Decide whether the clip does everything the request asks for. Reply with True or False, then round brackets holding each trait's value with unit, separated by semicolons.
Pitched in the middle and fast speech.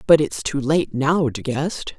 True (145 Hz; 210 wpm)